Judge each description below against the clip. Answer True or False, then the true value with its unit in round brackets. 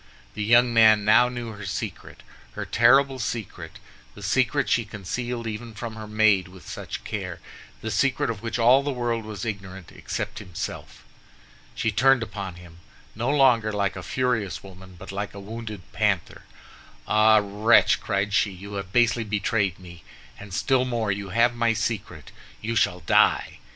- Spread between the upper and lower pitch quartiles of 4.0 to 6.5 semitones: False (3.0 semitones)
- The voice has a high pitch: False (110 Hz)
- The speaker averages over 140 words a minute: True (165 wpm)